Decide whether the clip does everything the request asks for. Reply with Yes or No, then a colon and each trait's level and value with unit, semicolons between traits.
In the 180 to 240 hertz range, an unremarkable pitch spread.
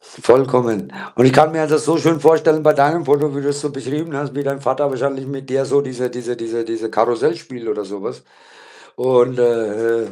No: low, 135 Hz; average, 3.4 semitones